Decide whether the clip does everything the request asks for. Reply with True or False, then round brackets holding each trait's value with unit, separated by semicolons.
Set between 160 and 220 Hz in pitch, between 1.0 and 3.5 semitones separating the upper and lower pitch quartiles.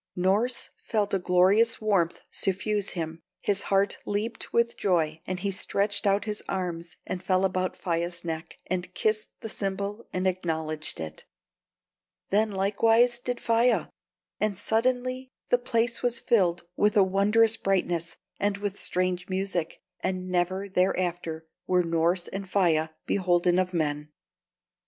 True (190 Hz; 3.1 semitones)